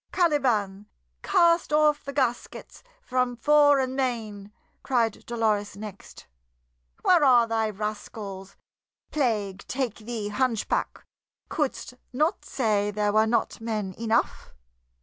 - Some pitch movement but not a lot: Yes, average, 4.2 semitones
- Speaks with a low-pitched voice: No, high, 230 Hz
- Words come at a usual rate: No, slow, 110 wpm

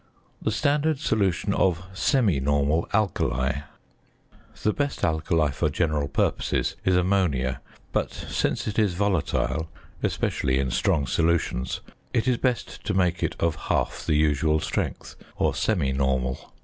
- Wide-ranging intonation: Yes, wide, 6.1 semitones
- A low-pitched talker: Yes, very low, 85 Hz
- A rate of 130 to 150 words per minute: Yes, slow, 135 wpm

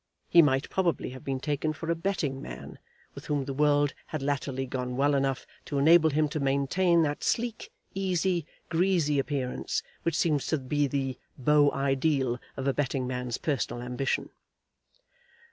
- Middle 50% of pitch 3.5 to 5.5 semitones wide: No, average, 3.0 semitones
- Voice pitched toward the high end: No, medium, 145 Hz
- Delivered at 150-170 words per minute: Yes, average, 160 wpm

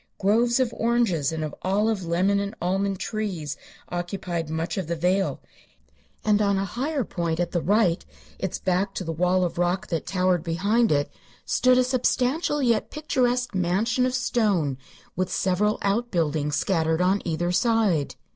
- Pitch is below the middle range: No, high, 190 Hz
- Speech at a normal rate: Yes, average, 160 wpm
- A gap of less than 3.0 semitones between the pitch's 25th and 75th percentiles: No, average, 4.6 semitones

